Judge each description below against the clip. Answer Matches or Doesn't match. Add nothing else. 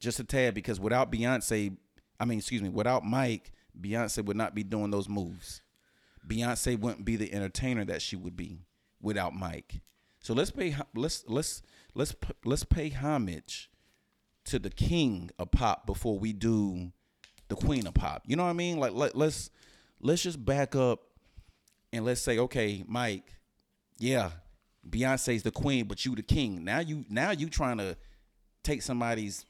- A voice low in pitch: Matches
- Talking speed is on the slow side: Doesn't match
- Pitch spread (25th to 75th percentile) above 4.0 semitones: Matches